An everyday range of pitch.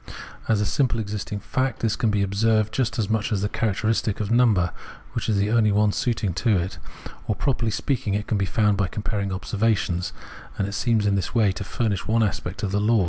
No: narrow, 2.1 semitones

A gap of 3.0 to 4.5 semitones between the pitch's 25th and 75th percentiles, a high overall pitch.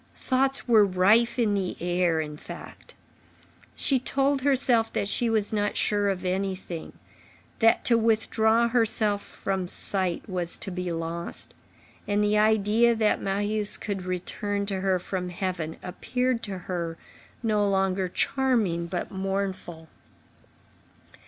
Yes: average, 3.4 semitones; high, 200 Hz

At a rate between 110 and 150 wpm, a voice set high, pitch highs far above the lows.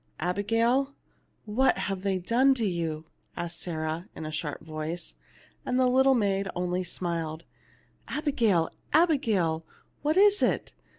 Yes: average, 140 wpm; high, 195 Hz; wide, 7.4 semitones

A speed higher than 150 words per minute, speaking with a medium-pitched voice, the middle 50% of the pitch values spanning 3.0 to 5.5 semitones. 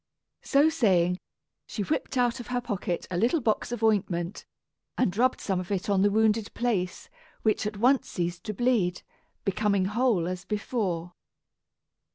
No: average, 160 wpm; high, 210 Hz; average, 4.7 semitones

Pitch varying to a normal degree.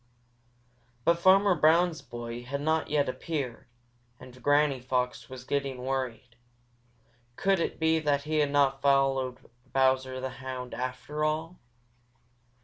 Yes: average, 3.2 semitones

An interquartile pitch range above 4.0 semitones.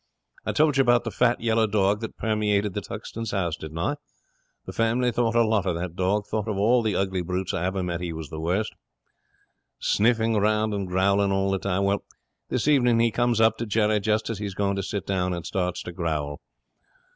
No: average, 3.4 semitones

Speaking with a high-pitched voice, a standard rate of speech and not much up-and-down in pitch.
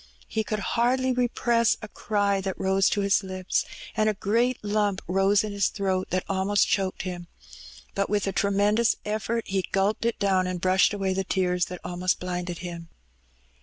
Yes: high, 195 Hz; average, 180 wpm; narrow, 2.2 semitones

